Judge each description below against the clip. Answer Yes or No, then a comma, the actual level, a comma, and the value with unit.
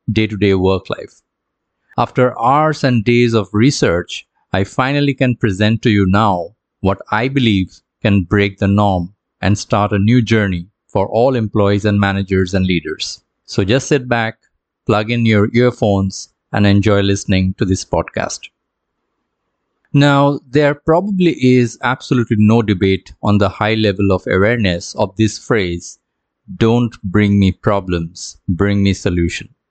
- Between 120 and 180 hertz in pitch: No, low, 105 Hz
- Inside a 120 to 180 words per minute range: Yes, average, 150 wpm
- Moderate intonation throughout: Yes, average, 3.6 semitones